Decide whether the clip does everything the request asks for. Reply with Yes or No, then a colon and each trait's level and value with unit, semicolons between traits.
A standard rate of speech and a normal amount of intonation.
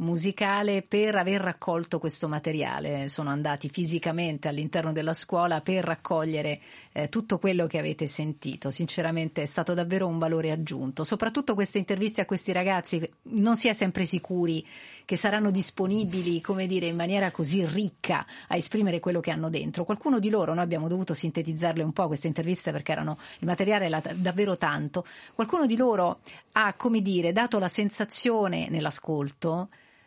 Yes: average, 160 wpm; average, 3.6 semitones